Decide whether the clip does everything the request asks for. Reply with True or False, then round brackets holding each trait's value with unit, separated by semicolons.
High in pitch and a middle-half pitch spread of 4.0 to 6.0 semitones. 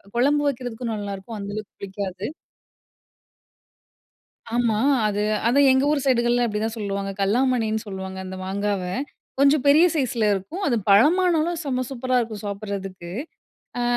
True (225 Hz; 4.7 semitones)